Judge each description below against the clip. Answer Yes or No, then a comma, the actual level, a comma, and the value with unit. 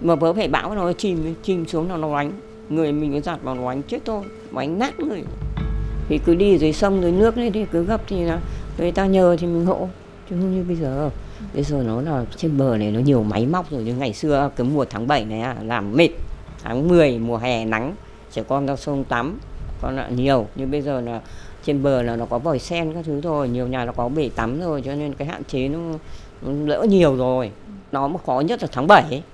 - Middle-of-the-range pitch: Yes, medium, 145 Hz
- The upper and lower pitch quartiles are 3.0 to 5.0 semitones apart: No, wide, 5.4 semitones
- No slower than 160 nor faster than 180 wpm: No, fast, 250 wpm